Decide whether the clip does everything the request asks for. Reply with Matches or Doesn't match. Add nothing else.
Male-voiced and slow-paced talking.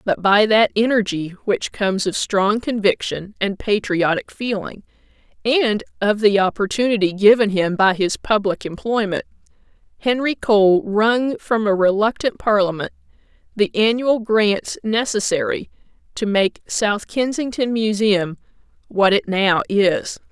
Doesn't match